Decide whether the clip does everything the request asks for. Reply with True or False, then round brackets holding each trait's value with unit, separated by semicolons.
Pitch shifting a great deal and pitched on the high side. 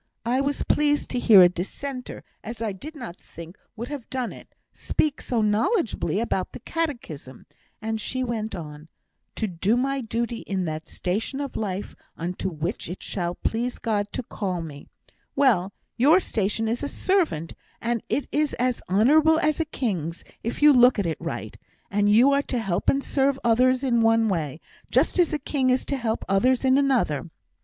True (5.9 semitones; 230 Hz)